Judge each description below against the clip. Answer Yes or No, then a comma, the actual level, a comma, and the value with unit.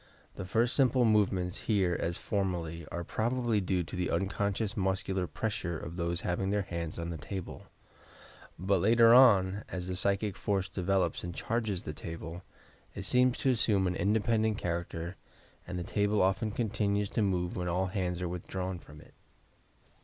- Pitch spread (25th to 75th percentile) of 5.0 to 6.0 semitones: No, average, 3.1 semitones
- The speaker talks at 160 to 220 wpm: Yes, average, 170 wpm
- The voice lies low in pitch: Yes, very low, 95 Hz